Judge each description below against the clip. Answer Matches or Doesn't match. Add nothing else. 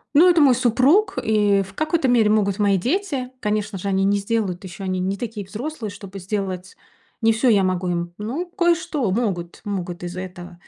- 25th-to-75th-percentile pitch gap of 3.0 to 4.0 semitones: Doesn't match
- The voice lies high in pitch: Matches